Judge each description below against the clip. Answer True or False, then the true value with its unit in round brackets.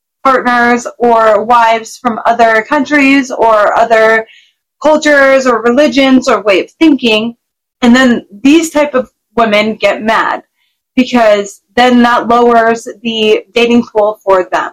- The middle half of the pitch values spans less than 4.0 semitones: True (2.9 semitones)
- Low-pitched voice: False (240 Hz)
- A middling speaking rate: False (130 wpm)